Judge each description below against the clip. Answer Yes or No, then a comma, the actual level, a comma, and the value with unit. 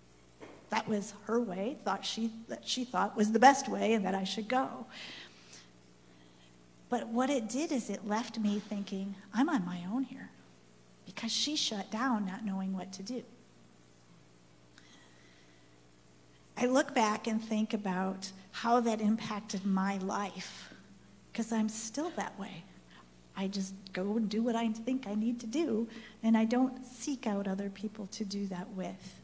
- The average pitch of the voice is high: Yes, high, 200 Hz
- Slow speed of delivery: No, average, 165 wpm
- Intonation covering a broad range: No, average, 4.3 semitones